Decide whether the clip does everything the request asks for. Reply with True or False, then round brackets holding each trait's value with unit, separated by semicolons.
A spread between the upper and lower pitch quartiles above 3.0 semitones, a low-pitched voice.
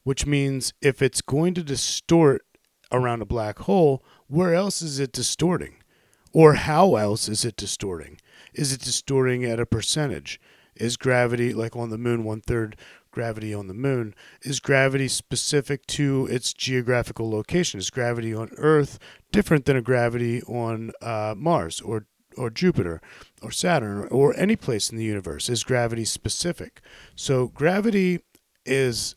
True (4.0 semitones; 125 Hz)